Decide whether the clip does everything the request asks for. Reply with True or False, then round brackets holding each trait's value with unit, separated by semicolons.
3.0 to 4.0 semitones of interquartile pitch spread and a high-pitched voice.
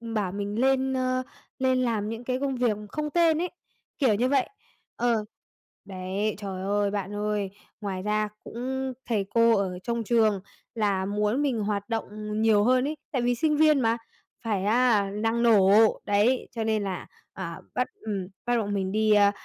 True (3.6 semitones; 220 Hz)